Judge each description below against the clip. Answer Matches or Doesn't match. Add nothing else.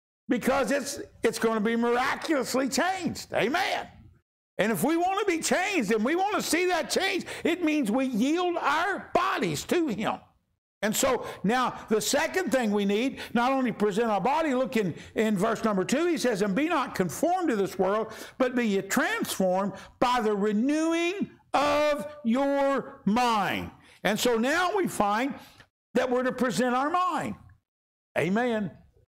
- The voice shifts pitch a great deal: Doesn't match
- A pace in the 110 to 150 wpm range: Doesn't match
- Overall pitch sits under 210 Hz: Doesn't match